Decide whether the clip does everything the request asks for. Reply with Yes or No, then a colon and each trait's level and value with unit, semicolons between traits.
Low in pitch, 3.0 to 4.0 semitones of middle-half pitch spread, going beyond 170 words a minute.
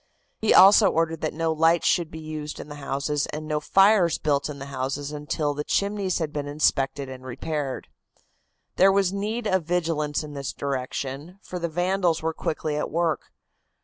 No: medium, 155 Hz; average, 3.4 semitones; average, 180 wpm